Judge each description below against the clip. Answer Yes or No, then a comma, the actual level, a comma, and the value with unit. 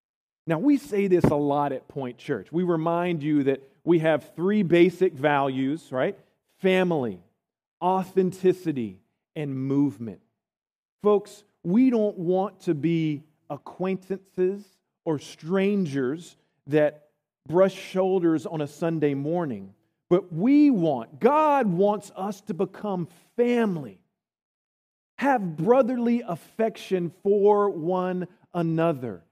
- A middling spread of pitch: Yes, average, 4.5 semitones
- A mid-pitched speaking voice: Yes, medium, 175 Hz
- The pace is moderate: No, slow, 110 wpm